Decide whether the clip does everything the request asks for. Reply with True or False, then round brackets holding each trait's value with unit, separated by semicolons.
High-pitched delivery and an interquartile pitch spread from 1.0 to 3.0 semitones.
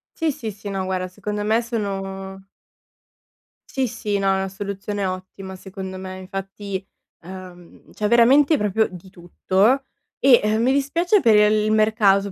True (200 Hz; 2.5 semitones)